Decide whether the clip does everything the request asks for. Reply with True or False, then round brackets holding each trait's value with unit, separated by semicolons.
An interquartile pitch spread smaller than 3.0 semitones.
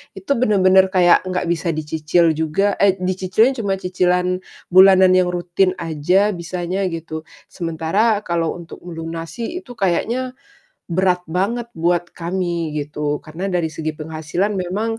True (2.6 semitones)